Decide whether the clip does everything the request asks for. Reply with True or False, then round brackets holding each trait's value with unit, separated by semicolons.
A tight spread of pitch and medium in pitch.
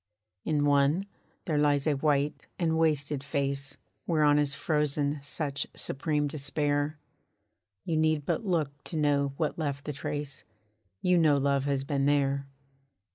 True (1.6 semitones; 145 Hz)